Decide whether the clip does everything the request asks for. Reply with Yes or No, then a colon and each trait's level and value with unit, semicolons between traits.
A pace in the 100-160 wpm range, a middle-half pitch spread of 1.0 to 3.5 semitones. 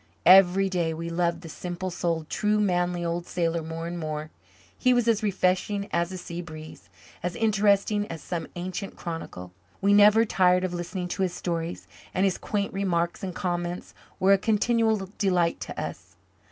No: average, 175 wpm; average, 2.7 semitones